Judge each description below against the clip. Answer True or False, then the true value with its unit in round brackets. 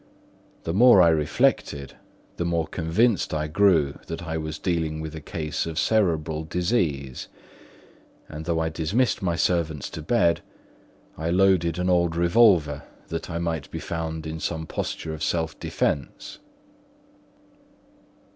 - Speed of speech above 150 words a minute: False (140 wpm)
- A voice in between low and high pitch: False (80 Hz)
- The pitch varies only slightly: True (1.9 semitones)